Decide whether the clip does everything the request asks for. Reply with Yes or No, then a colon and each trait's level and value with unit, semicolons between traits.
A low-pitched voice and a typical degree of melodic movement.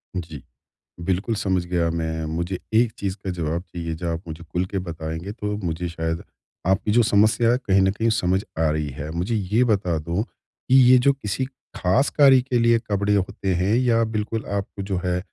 Yes: very low, 95 Hz; average, 4.4 semitones